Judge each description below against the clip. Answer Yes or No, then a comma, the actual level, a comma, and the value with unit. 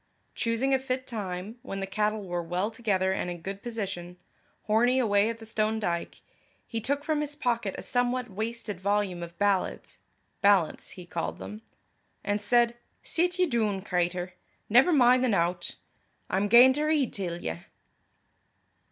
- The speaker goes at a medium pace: Yes, average, 160 wpm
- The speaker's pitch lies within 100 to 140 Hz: No, high, 215 Hz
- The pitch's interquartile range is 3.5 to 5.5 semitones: Yes, average, 4.5 semitones